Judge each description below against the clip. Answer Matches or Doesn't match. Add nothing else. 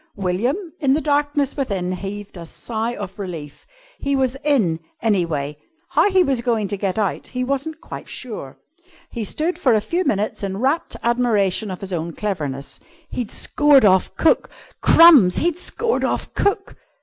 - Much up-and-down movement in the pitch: Matches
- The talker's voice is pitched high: Matches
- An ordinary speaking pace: Matches